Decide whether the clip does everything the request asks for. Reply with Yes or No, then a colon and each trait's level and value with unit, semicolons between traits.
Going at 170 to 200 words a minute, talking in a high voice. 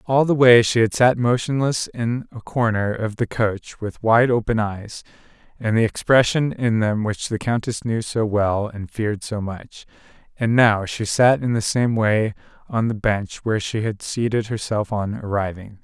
No: average, 190 wpm; low, 110 Hz